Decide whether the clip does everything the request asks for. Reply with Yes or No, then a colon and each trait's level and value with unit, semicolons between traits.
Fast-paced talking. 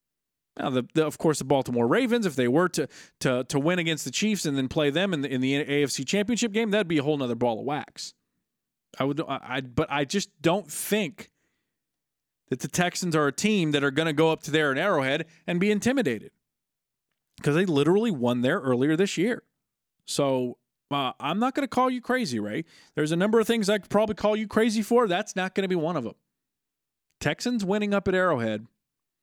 Yes: fast, 220 wpm